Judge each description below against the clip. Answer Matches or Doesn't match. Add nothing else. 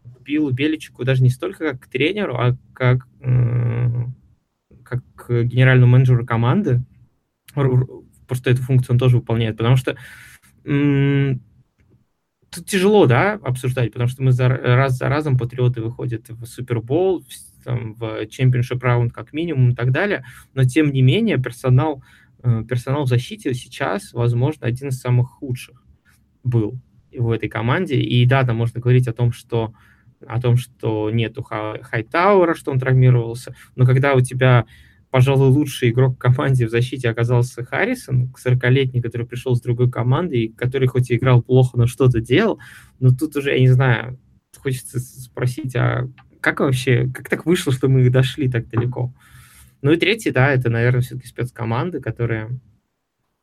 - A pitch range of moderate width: Doesn't match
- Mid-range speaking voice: Doesn't match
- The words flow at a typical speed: Matches